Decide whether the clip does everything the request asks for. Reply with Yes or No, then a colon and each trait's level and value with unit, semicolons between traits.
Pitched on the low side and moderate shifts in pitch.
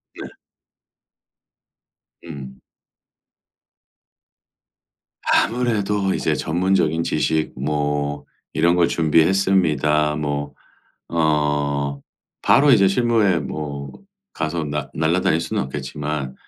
Yes: very low, 80 Hz; average, 3.9 semitones